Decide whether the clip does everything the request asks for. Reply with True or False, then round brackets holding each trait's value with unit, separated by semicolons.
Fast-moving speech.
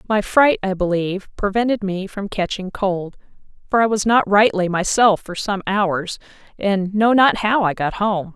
False (180 wpm)